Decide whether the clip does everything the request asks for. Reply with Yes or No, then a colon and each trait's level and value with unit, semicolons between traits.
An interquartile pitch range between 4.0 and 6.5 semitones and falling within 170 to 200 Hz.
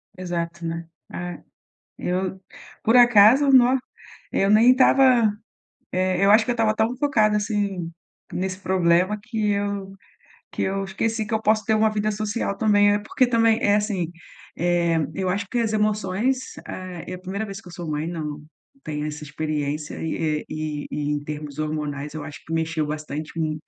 Yes: average, 4.9 semitones; high, 190 Hz